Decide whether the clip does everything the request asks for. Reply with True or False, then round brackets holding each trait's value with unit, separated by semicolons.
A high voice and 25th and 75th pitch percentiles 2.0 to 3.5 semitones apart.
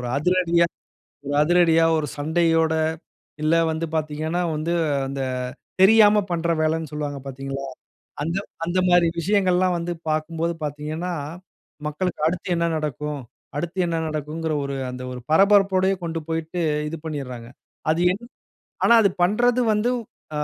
False (165 Hz; 2.9 semitones)